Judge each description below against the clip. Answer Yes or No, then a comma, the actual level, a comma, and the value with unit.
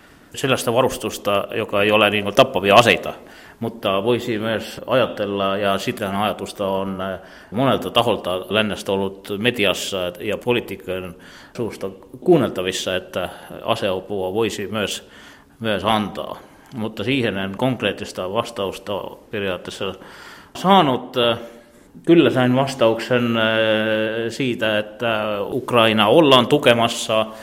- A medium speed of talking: Yes, average, 110 wpm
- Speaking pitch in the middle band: No, low, 110 Hz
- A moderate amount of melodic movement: Yes, average, 3.1 semitones